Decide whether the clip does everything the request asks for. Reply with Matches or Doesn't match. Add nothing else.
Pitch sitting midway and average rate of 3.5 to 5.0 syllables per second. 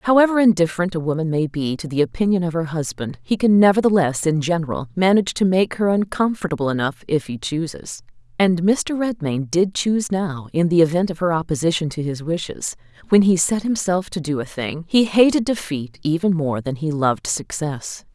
Doesn't match